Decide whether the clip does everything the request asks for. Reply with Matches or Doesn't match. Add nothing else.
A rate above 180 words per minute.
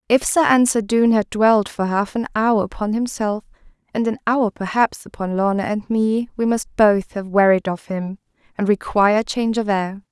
Matches